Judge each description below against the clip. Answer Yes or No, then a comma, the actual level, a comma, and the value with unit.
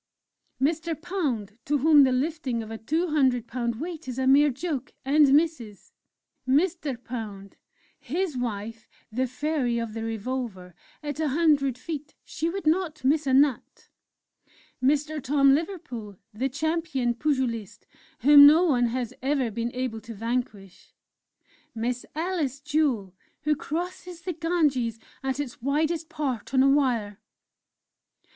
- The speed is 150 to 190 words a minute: No, average, 140 wpm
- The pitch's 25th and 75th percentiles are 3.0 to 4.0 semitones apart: No, average, 4.5 semitones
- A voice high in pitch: Yes, very high, 270 Hz